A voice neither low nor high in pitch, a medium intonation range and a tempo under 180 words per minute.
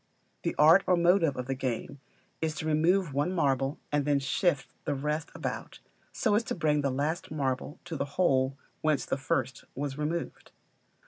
No: medium, 150 Hz; average, 3.3 semitones; average, 185 wpm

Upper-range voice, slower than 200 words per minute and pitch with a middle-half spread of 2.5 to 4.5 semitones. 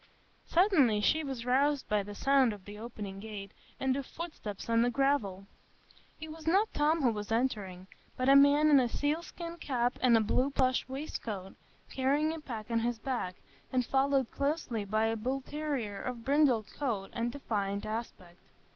No: very high, 250 Hz; average, 175 wpm; average, 4.9 semitones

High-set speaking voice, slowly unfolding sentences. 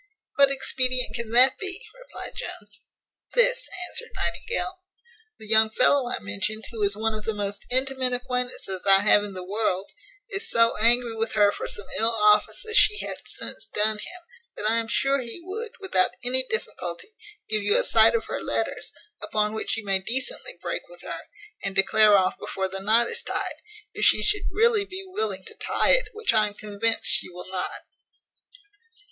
No: high, 230 Hz; average, 185 wpm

